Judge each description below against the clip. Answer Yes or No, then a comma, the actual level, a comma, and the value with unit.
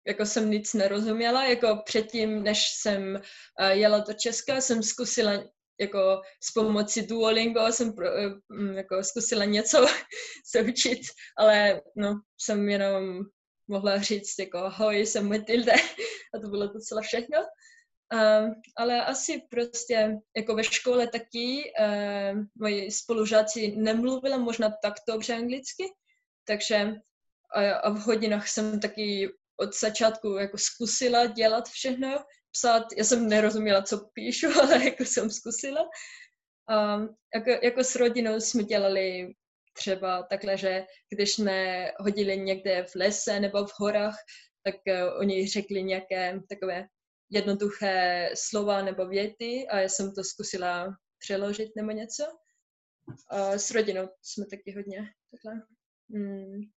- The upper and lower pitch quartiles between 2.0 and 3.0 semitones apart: Yes, average, 2.7 semitones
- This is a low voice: No, high, 215 Hz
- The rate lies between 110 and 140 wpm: Yes, average, 130 wpm